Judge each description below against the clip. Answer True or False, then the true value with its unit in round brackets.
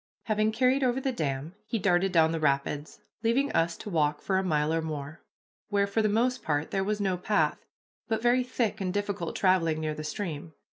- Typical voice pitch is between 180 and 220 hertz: True (190 Hz)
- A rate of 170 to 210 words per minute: True (205 wpm)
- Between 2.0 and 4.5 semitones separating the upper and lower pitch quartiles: False (5.6 semitones)